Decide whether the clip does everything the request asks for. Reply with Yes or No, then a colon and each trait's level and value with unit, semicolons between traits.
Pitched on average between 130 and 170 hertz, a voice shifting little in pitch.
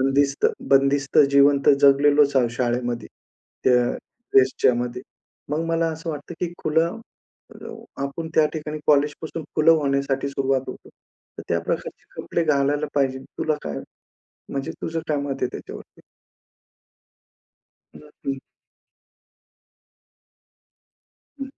Yes: medium, 140 Hz; narrow, 2.1 semitones